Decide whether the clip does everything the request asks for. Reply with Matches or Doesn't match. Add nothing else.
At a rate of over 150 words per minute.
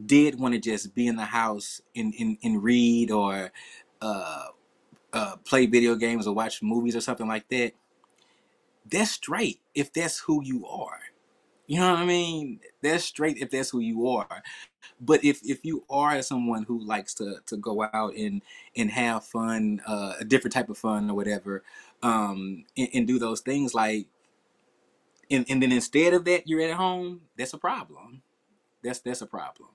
Matches